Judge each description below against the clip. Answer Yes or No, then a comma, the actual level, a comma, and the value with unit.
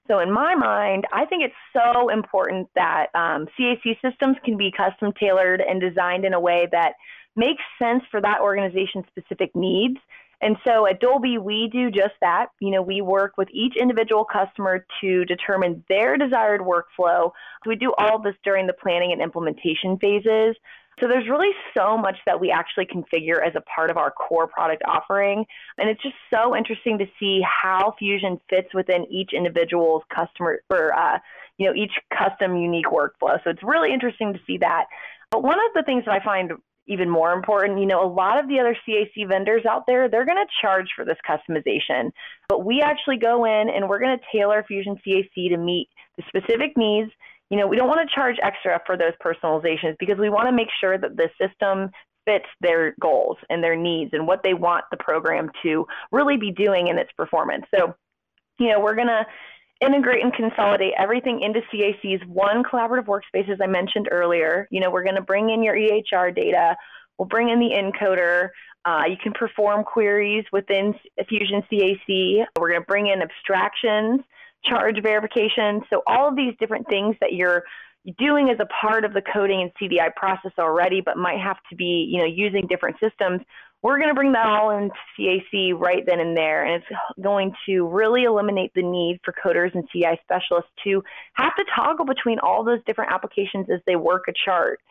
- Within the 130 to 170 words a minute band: No, average, 195 wpm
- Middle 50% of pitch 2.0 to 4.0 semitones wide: Yes, average, 3.6 semitones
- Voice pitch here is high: Yes, high, 200 Hz